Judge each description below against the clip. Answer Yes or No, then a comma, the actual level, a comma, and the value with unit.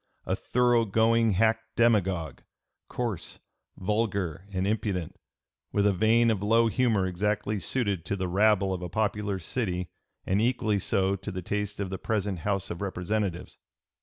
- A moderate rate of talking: Yes, average, 155 wpm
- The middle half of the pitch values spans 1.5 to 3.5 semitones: Yes, average, 2.9 semitones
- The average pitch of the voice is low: Yes, low, 100 Hz